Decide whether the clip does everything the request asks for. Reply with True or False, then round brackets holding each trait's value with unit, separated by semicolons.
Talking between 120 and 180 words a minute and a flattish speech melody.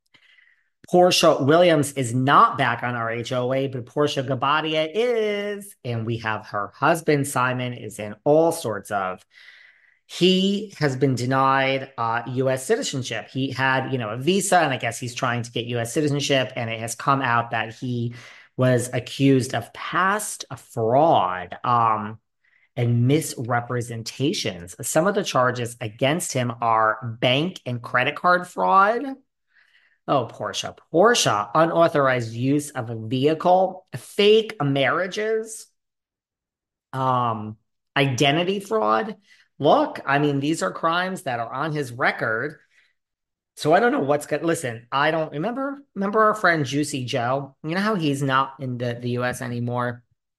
False (145 wpm; 4.9 semitones)